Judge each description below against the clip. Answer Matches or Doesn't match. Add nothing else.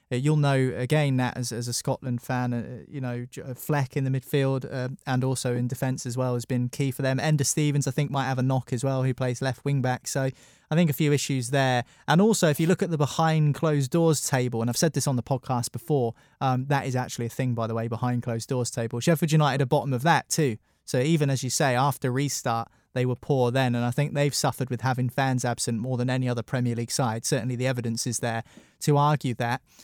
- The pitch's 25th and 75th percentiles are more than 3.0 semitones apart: Doesn't match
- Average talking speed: Doesn't match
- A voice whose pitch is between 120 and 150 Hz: Matches